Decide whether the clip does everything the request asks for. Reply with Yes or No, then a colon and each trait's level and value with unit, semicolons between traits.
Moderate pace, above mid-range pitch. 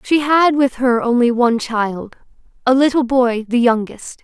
Yes: average, 170 wpm; very high, 250 Hz